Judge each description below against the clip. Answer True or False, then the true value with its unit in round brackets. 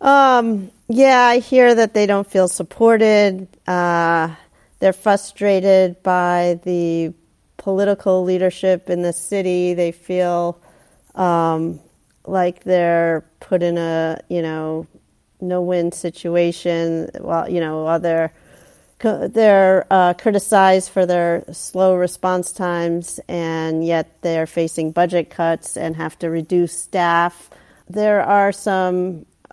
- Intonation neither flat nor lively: False (2.3 semitones)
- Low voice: False (180 Hz)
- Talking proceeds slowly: True (120 wpm)